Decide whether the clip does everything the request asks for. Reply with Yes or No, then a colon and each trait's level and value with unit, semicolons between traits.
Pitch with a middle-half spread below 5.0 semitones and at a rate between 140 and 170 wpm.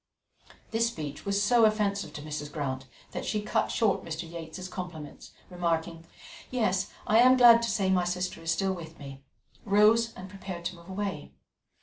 No: average, 4.4 semitones; average, 180 wpm